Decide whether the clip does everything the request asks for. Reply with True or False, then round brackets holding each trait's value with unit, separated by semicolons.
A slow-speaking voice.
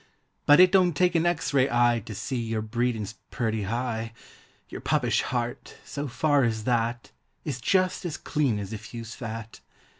False (175 wpm)